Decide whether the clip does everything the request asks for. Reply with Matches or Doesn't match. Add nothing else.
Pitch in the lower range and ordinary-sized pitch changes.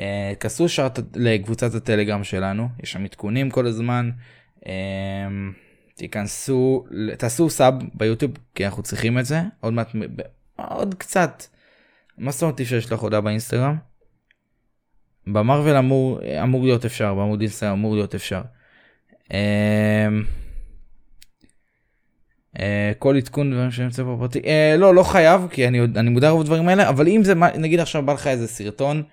Matches